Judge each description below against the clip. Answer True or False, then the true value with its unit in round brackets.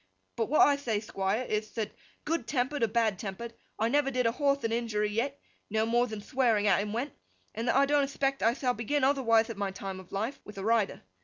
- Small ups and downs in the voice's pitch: False (4.2 semitones)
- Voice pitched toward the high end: True (230 Hz)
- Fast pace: True (235 wpm)